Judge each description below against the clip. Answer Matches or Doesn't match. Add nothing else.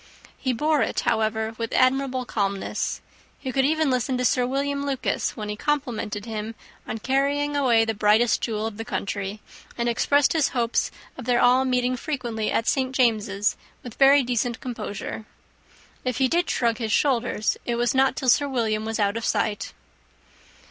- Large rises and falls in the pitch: Doesn't match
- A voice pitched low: Doesn't match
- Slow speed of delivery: Doesn't match